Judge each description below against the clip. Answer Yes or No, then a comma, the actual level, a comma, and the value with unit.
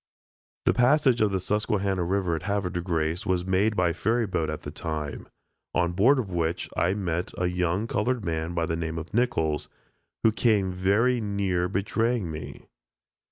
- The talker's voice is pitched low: Yes, very low, 95 Hz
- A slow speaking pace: No, average, 175 wpm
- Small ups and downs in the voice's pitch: No, average, 3.9 semitones